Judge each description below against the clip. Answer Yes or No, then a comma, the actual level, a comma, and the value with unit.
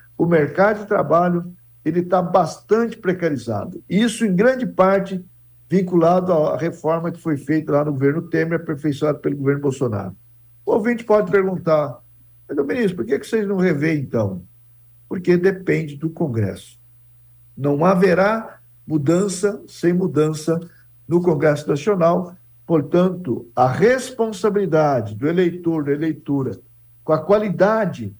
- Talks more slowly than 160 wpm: Yes, average, 130 wpm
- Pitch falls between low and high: Yes, medium, 165 Hz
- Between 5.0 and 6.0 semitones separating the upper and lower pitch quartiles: Yes, wide, 5.6 semitones